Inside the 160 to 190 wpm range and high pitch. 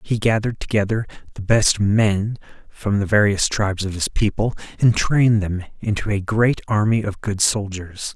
No: average, 170 wpm; low, 105 Hz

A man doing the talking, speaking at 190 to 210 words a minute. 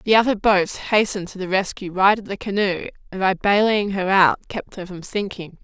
No: female; average, 200 wpm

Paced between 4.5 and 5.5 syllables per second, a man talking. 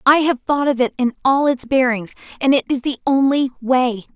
No: 5.2 syllables/s; female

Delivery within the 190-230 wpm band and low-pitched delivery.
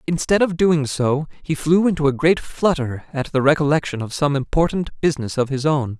No: average, 200 wpm; medium, 150 Hz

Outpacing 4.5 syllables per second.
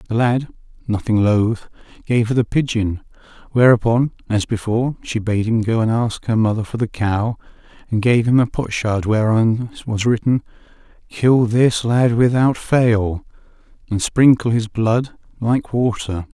No: 4.4 syllables/s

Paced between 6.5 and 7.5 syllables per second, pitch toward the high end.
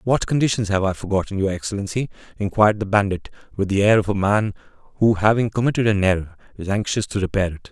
No: 6.6 syllables/s; low, 100 Hz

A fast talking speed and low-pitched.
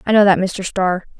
No: fast, 250 wpm; high, 190 Hz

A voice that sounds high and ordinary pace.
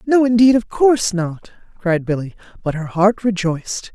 Yes: high, 200 Hz; average, 165 wpm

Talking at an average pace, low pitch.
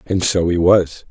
No: fast, 215 wpm; very low, 90 Hz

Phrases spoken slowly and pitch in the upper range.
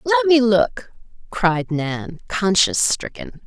Yes: slow, 120 wpm; high, 215 Hz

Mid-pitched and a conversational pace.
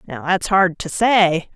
Yes: medium, 180 Hz; average, 195 wpm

